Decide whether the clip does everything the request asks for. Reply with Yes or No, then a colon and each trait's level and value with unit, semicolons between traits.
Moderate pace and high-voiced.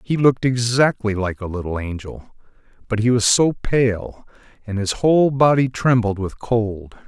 No: average, 160 wpm; low, 115 Hz